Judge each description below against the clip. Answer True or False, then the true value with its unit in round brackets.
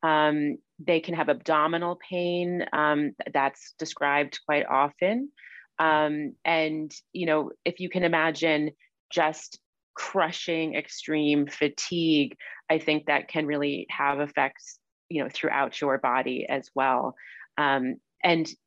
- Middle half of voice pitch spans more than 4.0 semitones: False (2.4 semitones)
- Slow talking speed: True (120 wpm)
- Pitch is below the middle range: False (155 Hz)